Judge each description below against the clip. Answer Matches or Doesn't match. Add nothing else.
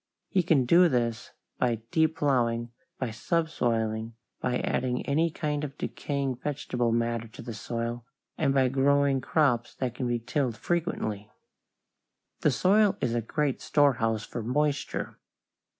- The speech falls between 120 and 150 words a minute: Matches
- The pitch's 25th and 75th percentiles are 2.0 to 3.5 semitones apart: Doesn't match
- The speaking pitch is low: Matches